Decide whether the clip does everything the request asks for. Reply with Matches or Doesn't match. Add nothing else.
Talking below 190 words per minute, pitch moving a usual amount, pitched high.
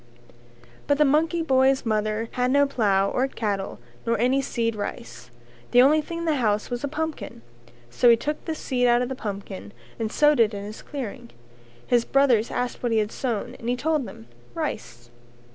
Doesn't match